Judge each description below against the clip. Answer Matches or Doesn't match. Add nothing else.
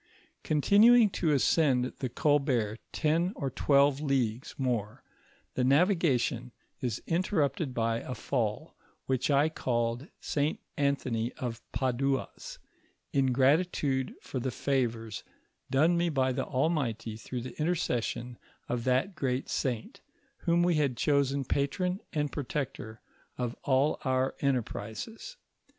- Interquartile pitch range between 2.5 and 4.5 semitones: Matches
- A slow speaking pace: Matches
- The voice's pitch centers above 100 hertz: Matches